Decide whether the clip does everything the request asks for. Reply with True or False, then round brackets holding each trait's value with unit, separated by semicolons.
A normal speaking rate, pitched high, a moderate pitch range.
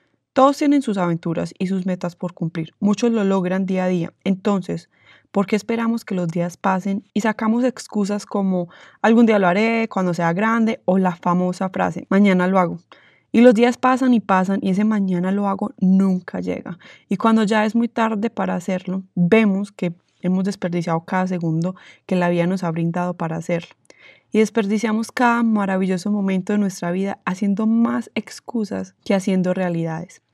True (180 wpm; 195 Hz; 3.3 semitones)